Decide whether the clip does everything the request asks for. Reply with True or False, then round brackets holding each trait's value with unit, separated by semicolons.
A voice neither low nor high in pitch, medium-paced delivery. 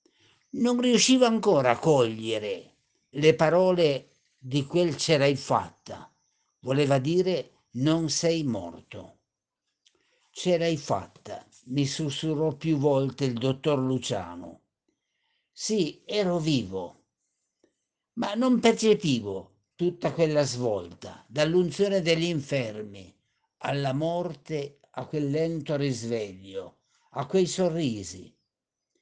False (150 Hz; 100 wpm)